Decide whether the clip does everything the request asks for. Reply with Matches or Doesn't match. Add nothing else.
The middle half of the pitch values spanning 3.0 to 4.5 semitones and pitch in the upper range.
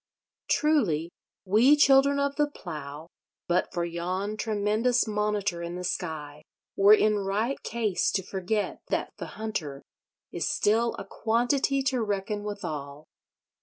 Doesn't match